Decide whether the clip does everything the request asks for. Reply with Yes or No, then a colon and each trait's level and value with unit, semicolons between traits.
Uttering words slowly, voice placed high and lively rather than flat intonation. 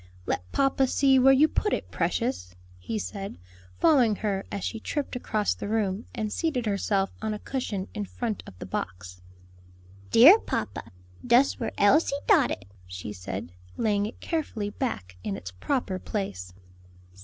No: average, 160 wpm; high, 210 Hz; wide, 5.9 semitones